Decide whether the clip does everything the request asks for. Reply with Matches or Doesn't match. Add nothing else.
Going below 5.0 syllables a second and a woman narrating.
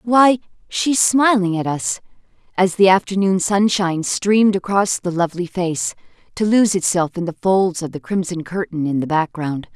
Matches